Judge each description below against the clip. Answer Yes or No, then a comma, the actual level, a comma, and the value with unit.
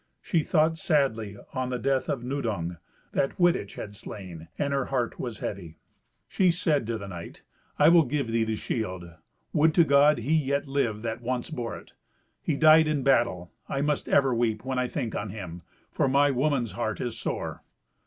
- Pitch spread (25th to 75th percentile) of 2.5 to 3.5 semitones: No, average, 4.7 semitones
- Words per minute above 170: Yes, average, 190 wpm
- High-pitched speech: No, low, 125 Hz